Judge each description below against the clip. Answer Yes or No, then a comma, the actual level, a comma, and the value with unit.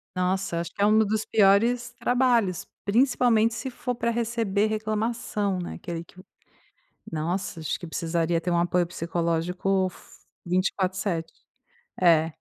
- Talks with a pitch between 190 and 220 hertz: Yes, high, 195 Hz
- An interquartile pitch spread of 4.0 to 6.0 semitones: Yes, average, 4.3 semitones